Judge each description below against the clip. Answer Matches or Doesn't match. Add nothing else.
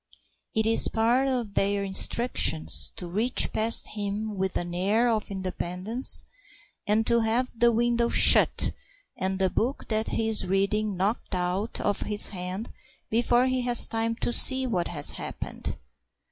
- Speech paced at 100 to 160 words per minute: Matches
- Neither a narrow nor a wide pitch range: Matches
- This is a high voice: Matches